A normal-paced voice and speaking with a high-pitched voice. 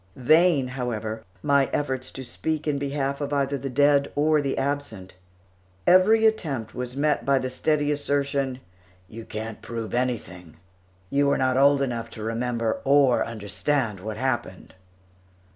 No: average, 145 wpm; low, 135 Hz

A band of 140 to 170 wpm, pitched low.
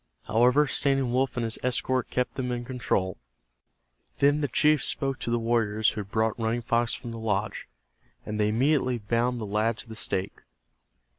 No: average, 180 wpm; low, 120 Hz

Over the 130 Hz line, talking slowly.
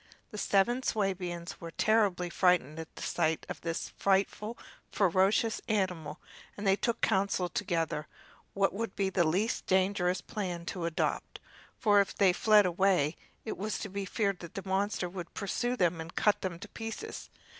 No: high, 190 Hz; average, 165 wpm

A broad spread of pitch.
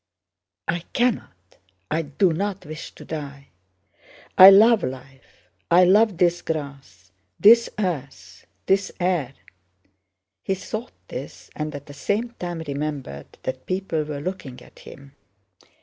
Yes: wide, 5.7 semitones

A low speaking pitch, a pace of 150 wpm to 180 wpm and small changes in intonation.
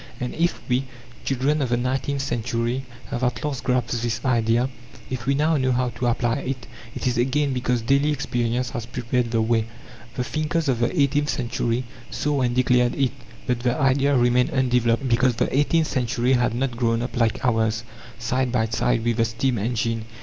No: low, 125 Hz; average, 190 wpm; narrow, 2.2 semitones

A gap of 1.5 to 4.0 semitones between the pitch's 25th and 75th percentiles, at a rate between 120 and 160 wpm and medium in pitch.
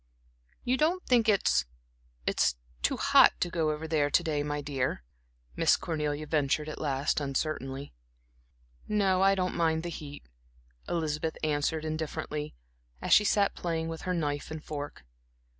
Yes: average, 2.9 semitones; average, 150 wpm; medium, 155 Hz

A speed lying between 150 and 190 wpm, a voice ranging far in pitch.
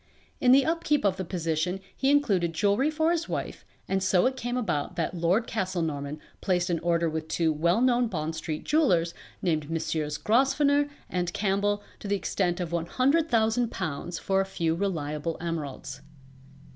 Yes: average, 160 wpm; wide, 6.3 semitones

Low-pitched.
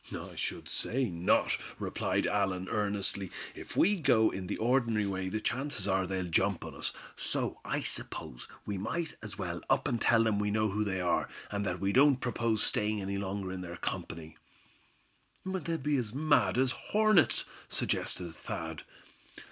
Yes: low, 105 Hz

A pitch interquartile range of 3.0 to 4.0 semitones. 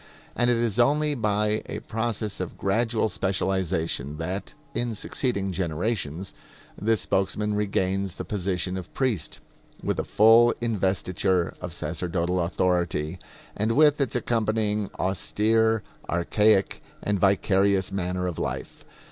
Yes: average, 3.4 semitones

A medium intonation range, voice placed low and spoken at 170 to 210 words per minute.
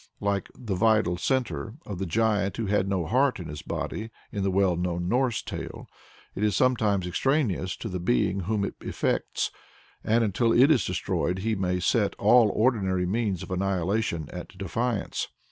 Yes: average, 3.7 semitones; low, 100 Hz; average, 175 wpm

